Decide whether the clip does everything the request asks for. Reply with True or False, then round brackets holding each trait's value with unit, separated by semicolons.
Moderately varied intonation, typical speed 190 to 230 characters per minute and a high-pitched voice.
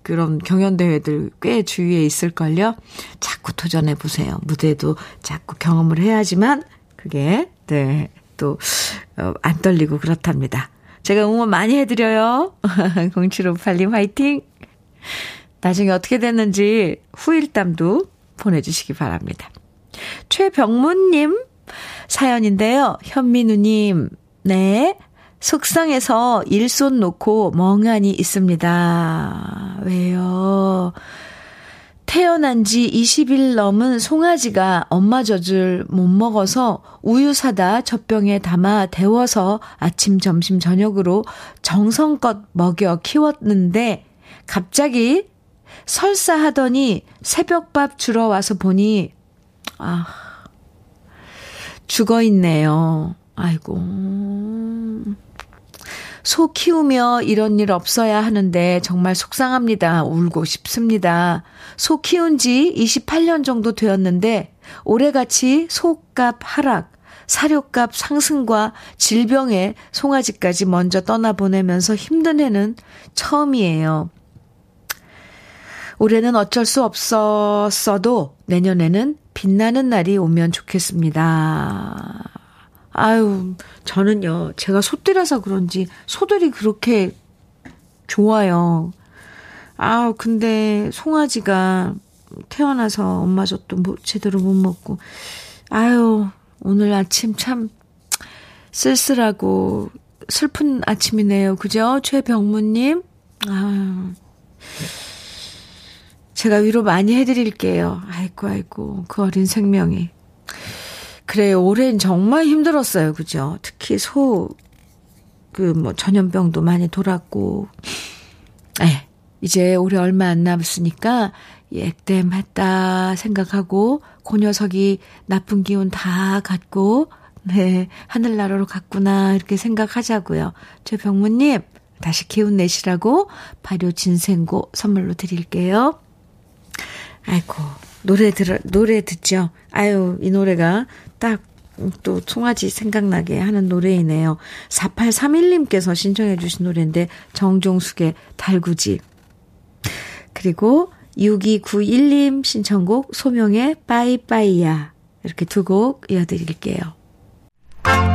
True (4.3 semitones; 215 characters per minute; 200 Hz)